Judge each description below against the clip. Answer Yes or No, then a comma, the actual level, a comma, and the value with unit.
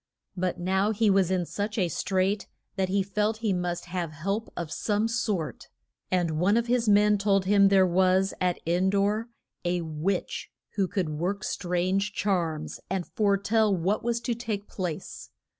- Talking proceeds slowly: No, average, 175 wpm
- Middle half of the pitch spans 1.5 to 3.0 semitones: Yes, narrow, 2.6 semitones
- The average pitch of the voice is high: Yes, high, 195 Hz